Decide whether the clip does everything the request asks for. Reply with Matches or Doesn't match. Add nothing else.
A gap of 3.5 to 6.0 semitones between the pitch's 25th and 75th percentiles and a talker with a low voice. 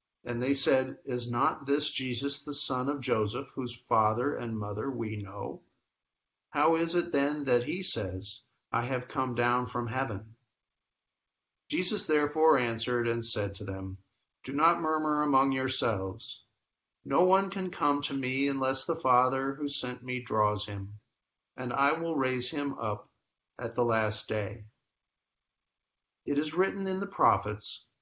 Matches